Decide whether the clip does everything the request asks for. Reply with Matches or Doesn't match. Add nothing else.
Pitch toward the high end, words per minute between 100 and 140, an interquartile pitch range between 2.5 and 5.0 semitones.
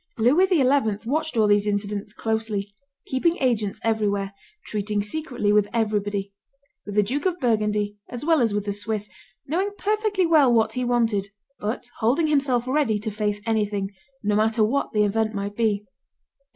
Doesn't match